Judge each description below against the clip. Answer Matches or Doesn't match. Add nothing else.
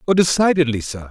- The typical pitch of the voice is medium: Matches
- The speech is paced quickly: Doesn't match